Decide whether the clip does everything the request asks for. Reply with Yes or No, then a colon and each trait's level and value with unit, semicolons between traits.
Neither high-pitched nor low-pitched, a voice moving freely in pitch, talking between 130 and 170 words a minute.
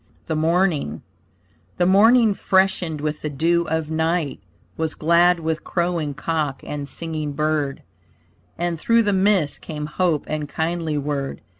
No: medium, 160 Hz; narrow, 2.6 semitones; average, 140 wpm